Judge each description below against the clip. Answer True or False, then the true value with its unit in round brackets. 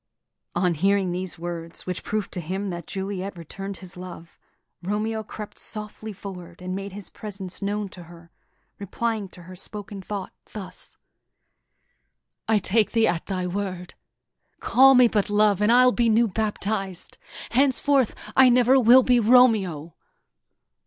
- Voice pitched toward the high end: True (200 Hz)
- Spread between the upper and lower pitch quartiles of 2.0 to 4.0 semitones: True (3.3 semitones)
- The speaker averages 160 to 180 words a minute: False (145 wpm)